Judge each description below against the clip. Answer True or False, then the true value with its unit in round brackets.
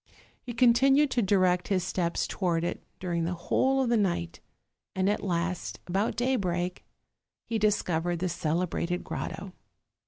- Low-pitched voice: False (185 Hz)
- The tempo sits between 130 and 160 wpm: True (150 wpm)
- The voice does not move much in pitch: False (4.4 semitones)